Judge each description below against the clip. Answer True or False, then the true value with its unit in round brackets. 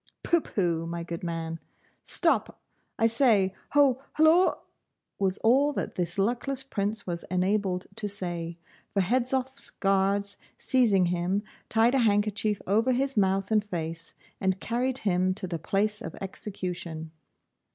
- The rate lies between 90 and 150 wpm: True (140 wpm)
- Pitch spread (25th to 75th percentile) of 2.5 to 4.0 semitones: False (4.6 semitones)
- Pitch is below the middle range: False (200 Hz)